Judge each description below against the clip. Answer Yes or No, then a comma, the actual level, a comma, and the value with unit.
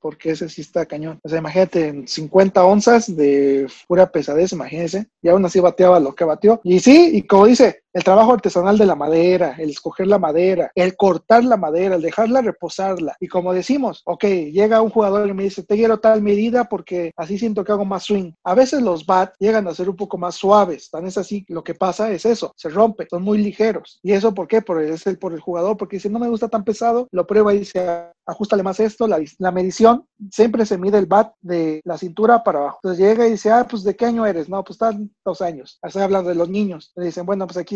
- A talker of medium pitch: No, high, 195 Hz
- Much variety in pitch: No, average, 3.6 semitones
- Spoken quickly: Yes, fast, 240 wpm